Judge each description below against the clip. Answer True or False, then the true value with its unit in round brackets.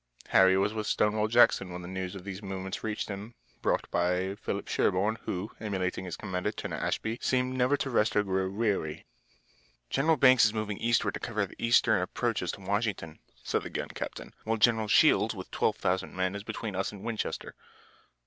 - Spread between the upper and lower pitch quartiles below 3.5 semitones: True (3.0 semitones)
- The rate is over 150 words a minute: True (185 wpm)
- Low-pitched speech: True (105 Hz)